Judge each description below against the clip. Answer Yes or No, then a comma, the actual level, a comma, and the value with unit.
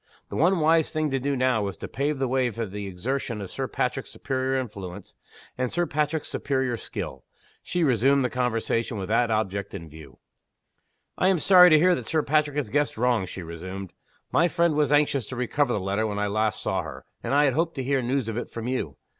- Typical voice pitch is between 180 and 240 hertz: No, low, 125 Hz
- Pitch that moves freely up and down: Yes, wide, 5.8 semitones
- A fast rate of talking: Yes, fast, 220 wpm